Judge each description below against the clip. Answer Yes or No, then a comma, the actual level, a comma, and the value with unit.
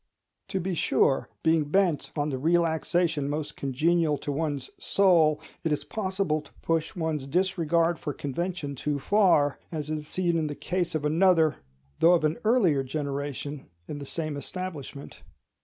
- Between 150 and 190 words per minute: Yes, average, 155 wpm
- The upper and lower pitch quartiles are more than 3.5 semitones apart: No, average, 3.1 semitones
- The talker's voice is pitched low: No, medium, 155 Hz